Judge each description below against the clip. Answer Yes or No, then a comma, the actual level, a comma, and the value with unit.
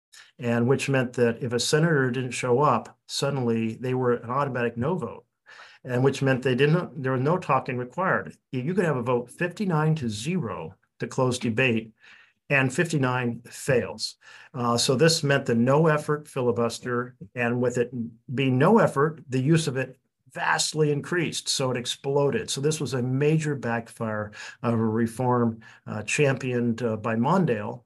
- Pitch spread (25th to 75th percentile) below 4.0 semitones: Yes, average, 3.3 semitones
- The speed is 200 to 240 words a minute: No, average, 170 wpm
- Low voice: Yes, low, 130 Hz